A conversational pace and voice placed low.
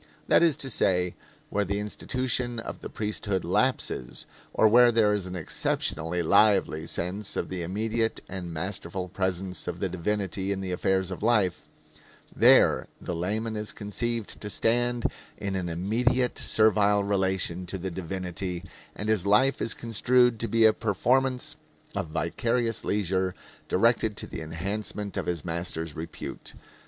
Yes: average, 150 wpm; low, 100 Hz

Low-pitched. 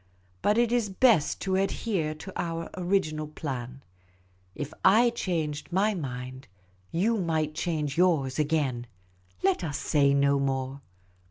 No: medium, 155 Hz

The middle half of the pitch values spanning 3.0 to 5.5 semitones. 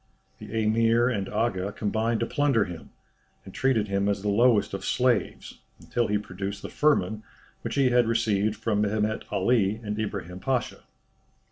No: narrow, 2.6 semitones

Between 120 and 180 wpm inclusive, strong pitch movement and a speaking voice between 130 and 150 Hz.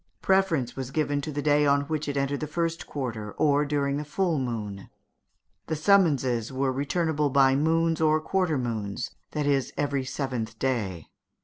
No: average, 170 wpm; average, 3.1 semitones; medium, 140 Hz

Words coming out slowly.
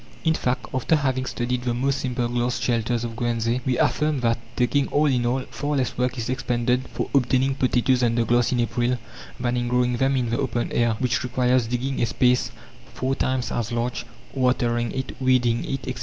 No: average, 200 wpm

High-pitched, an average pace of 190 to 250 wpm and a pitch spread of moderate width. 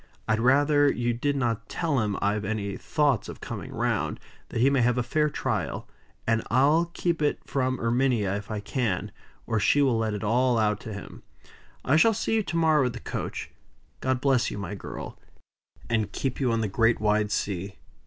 No: low, 120 Hz; average, 200 wpm; average, 4.5 semitones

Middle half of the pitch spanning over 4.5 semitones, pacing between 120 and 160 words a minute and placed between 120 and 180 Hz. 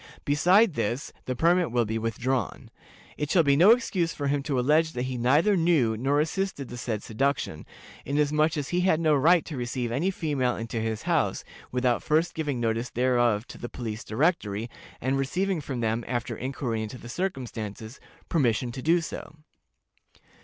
No: average, 5.1 semitones; average, 175 wpm; low, 135 Hz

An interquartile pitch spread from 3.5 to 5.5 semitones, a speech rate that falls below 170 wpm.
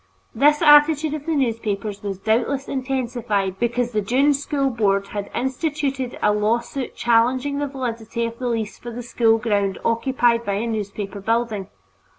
Yes: average, 4.1 semitones; average, 160 wpm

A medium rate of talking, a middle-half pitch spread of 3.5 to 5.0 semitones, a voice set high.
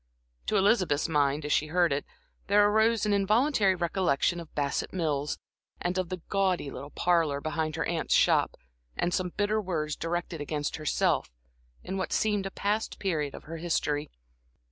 No: average, 165 wpm; average, 4.6 semitones; medium, 175 Hz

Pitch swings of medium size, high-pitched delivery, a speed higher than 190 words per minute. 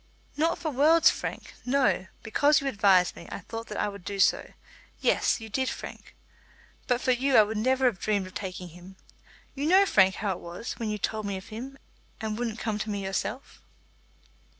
Yes: average, 5.0 semitones; high, 220 Hz; average, 200 wpm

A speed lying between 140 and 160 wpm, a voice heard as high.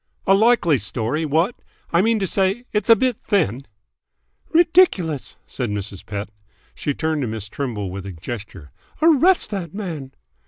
No: average, 155 wpm; medium, 160 Hz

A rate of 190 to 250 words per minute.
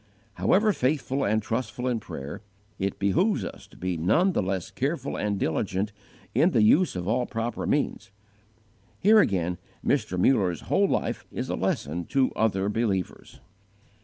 No: average, 155 wpm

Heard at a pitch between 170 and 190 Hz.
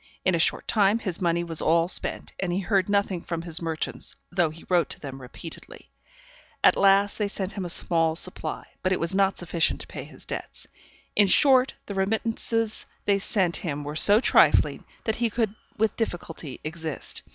Yes: medium, 185 Hz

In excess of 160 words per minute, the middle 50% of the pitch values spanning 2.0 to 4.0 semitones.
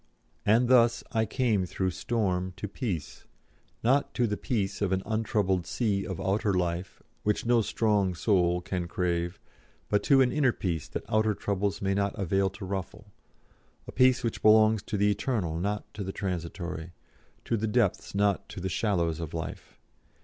Yes: average, 170 wpm; average, 3.4 semitones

